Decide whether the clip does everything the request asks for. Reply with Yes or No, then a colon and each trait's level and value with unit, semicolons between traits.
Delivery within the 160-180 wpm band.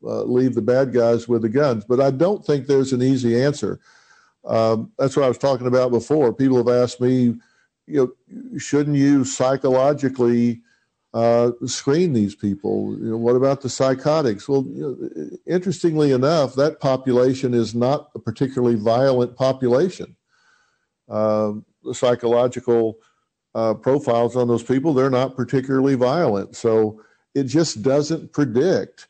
No: average, 150 wpm